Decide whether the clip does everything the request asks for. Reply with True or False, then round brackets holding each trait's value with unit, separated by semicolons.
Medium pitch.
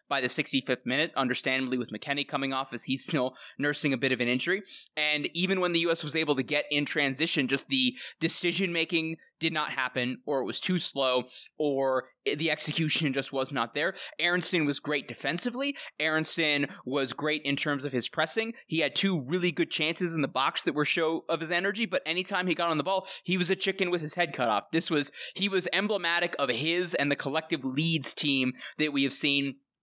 True (155 Hz)